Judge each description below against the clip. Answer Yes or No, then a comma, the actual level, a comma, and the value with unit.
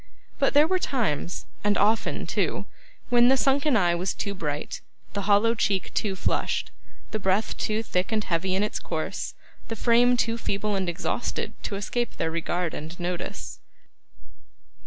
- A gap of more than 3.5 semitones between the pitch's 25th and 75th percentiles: Yes, average, 4.4 semitones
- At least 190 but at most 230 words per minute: No, average, 160 wpm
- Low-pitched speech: No, high, 205 Hz